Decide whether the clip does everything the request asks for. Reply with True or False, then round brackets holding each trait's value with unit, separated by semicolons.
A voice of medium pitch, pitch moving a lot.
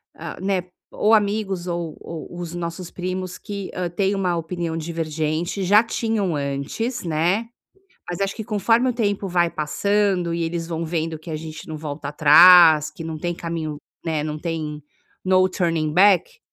False (175 Hz; 3.4 semitones)